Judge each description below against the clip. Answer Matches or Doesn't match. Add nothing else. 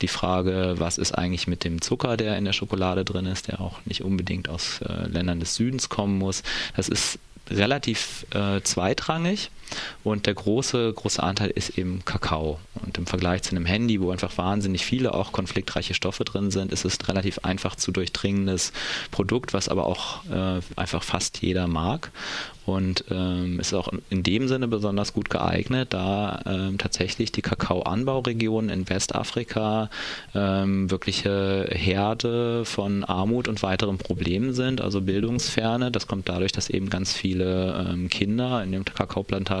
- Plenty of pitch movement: Doesn't match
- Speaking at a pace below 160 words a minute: Doesn't match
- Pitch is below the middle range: Matches